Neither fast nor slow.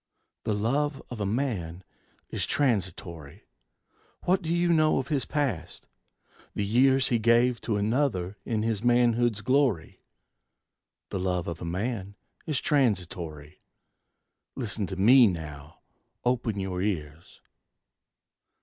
No: slow, 120 wpm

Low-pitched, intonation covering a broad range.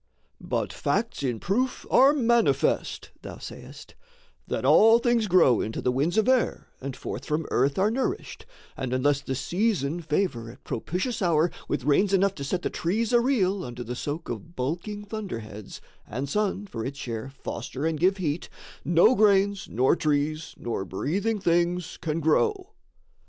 No: medium, 170 Hz; wide, 7.0 semitones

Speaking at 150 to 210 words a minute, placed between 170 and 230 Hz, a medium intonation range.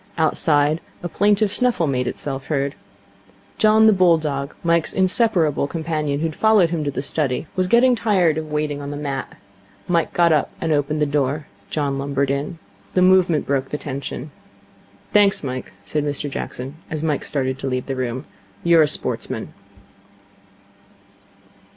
No: average, 165 wpm; medium, 150 Hz; average, 3.5 semitones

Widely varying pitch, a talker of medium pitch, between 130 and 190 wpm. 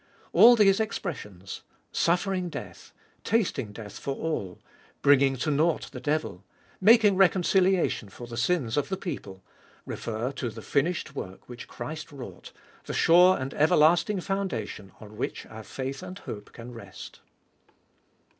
Yes: wide, 8.0 semitones; medium, 145 Hz; average, 145 wpm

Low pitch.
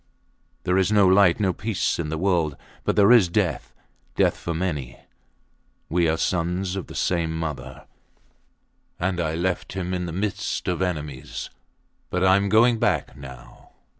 Yes: very low, 90 Hz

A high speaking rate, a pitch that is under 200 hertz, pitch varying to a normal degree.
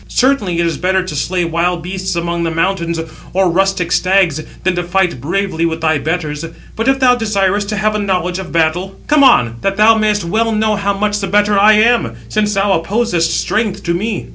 Yes: fast, 210 wpm; high, 190 Hz; average, 3.7 semitones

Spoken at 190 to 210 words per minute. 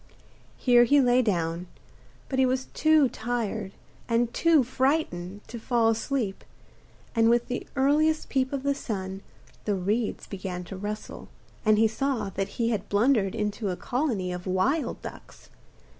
No: average, 155 wpm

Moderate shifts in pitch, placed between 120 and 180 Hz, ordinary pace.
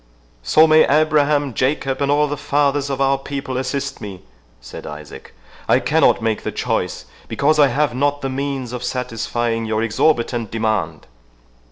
Yes: average, 4.0 semitones; low, 135 Hz; average, 160 wpm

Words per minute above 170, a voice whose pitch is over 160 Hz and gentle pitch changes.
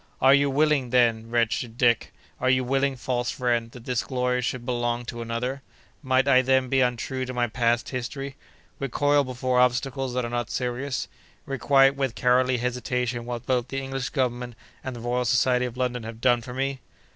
No: average, 180 wpm; low, 125 Hz; narrow, 1.6 semitones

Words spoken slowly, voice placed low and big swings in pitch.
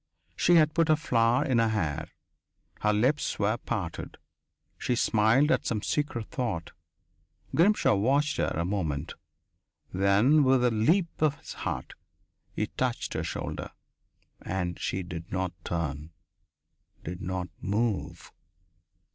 Yes: slow, 130 wpm; low, 110 Hz; wide, 6.8 semitones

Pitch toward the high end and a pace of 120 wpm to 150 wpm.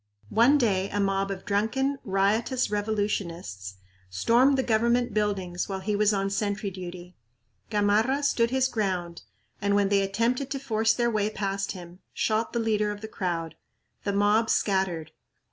No: high, 205 Hz; average, 160 wpm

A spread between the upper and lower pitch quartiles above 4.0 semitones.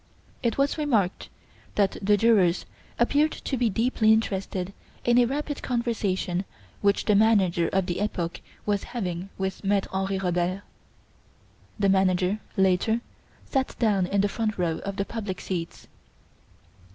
No: average, 3.5 semitones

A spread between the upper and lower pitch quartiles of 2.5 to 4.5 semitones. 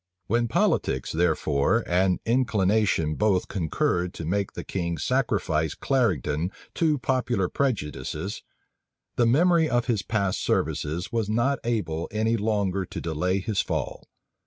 No: average, 5.1 semitones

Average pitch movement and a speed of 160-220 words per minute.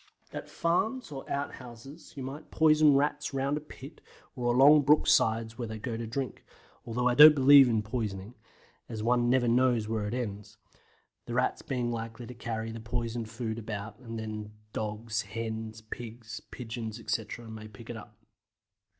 Yes: average, 3.0 semitones; average, 175 wpm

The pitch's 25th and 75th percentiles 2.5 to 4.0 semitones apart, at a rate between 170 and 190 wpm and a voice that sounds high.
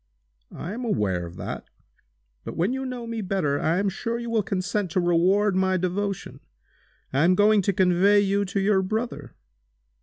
Yes: average, 2.8 semitones; average, 180 wpm; high, 195 Hz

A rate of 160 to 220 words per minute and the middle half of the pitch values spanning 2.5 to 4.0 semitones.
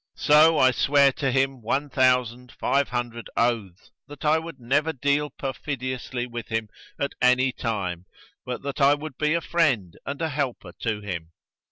Yes: average, 170 wpm; average, 3.5 semitones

